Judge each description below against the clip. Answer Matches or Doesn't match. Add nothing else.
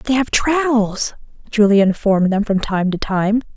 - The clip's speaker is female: Matches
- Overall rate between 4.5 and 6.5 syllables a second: Matches